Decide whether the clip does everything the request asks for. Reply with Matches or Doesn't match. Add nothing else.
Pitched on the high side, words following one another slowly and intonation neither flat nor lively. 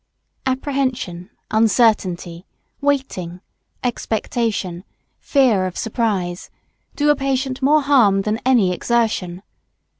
Doesn't match